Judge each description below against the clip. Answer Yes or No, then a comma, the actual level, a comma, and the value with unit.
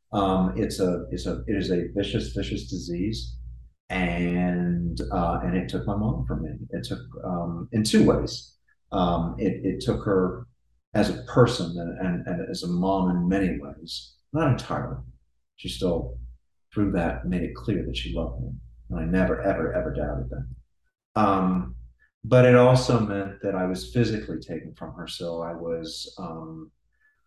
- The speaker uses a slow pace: No, average, 175 wpm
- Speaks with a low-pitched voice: Yes, very low, 90 Hz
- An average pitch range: No, wide, 5.8 semitones